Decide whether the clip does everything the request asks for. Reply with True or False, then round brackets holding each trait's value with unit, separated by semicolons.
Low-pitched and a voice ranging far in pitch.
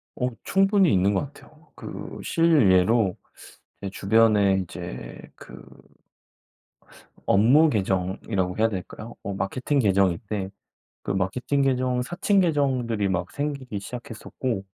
True (115 Hz; 6.1 semitones)